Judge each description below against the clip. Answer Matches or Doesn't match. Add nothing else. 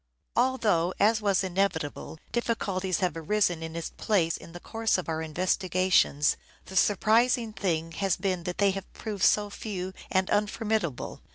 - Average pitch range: Matches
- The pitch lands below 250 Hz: Matches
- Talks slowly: Doesn't match